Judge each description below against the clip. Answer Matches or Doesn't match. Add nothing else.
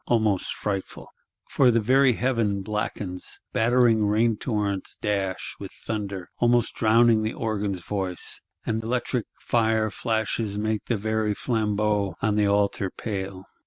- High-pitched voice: Doesn't match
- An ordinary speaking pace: Doesn't match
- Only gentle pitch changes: Matches